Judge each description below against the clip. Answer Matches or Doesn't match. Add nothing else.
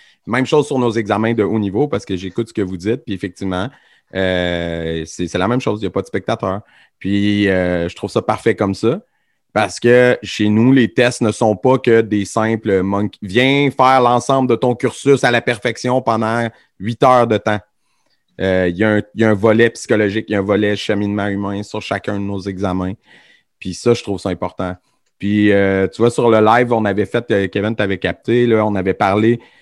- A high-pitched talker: Doesn't match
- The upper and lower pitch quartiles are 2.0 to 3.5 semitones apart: Matches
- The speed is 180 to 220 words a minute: Matches